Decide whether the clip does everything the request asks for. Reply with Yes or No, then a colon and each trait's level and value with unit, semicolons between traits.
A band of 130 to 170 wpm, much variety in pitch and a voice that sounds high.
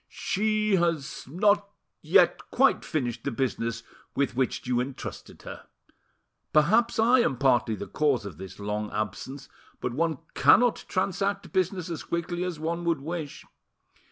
No: average, 145 wpm; wide, 6.8 semitones; medium, 155 Hz